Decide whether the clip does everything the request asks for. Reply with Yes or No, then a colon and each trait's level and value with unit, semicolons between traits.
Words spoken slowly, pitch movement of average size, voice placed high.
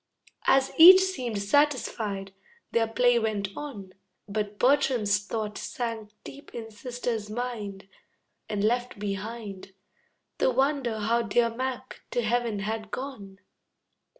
Yes: slow, 120 wpm; average, 3.2 semitones; high, 225 Hz